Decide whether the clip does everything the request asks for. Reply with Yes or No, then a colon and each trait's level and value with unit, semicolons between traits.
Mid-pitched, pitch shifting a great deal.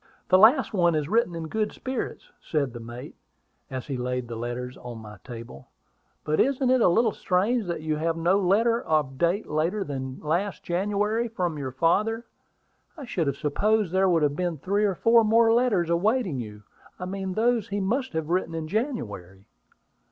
Yes: medium, 175 Hz; wide, 7.1 semitones